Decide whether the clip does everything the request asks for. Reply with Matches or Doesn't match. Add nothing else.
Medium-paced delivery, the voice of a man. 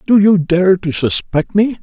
Matches